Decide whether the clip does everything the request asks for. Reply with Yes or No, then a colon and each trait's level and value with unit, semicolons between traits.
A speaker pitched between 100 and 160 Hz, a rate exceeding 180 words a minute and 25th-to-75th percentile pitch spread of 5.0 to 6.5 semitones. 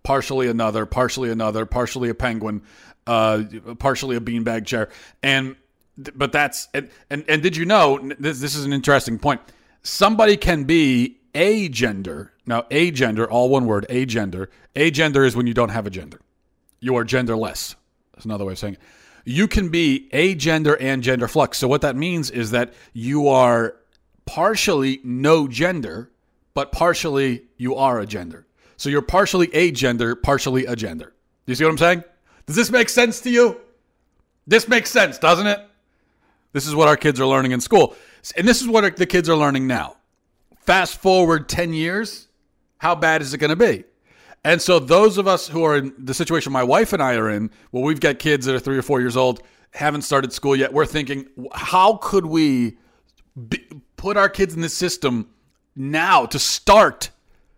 Yes: medium, 140 Hz; average, 190 wpm; wide, 5.4 semitones